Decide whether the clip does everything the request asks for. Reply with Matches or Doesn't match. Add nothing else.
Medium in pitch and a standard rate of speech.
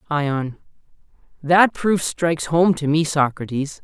Doesn't match